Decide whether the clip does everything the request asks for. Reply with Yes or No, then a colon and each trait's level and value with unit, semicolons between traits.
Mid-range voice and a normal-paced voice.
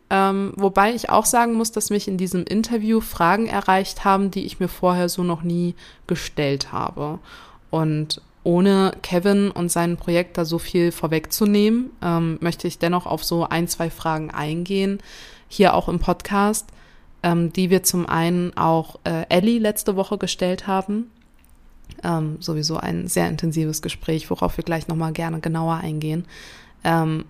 Yes: medium, 175 Hz; average, 160 wpm